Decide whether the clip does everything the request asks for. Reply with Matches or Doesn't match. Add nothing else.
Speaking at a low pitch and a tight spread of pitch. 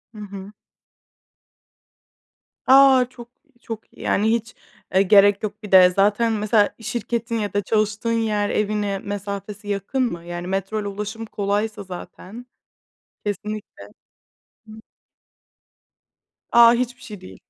Doesn't match